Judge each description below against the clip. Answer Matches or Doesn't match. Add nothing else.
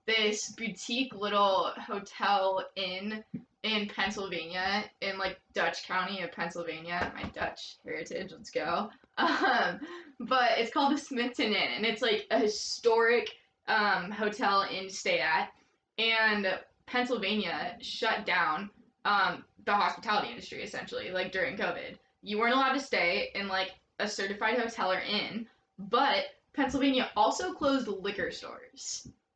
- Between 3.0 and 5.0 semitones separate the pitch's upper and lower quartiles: Matches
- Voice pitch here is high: Matches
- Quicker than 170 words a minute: Doesn't match